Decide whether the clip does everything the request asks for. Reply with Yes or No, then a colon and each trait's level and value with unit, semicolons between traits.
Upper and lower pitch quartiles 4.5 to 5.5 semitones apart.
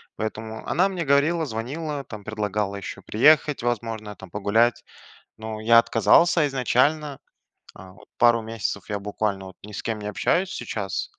Yes: average, 5.1 semitones